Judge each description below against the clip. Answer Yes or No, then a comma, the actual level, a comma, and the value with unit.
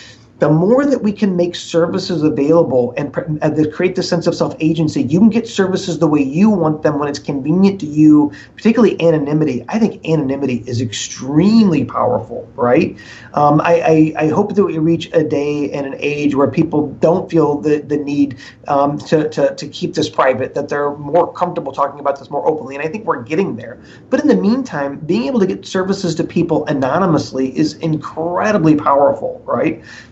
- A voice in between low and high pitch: Yes, medium, 155 Hz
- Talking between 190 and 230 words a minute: Yes, average, 195 wpm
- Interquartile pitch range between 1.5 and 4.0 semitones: Yes, average, 3.5 semitones